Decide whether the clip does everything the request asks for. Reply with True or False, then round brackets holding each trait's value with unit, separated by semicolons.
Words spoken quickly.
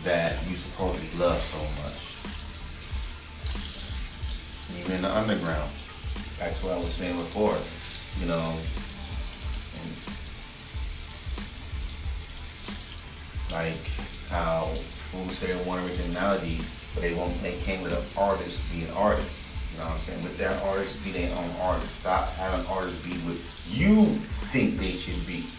False (140 wpm)